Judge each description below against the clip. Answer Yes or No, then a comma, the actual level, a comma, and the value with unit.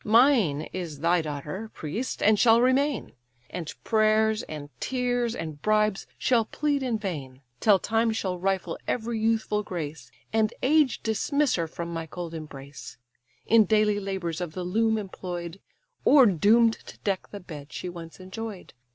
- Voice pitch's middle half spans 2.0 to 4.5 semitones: No, average, 5.0 semitones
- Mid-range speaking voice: No, high, 205 Hz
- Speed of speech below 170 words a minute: Yes, average, 155 wpm